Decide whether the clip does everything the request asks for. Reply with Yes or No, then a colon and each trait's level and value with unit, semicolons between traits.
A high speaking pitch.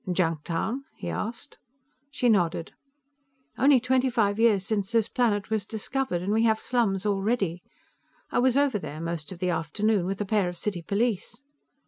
Yes: high, 210 Hz